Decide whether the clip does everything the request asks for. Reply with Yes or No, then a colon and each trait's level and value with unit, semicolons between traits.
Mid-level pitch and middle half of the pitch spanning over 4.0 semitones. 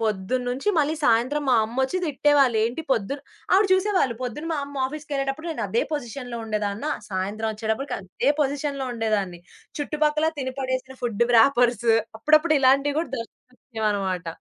No: very high, 260 Hz; average, 4.6 semitones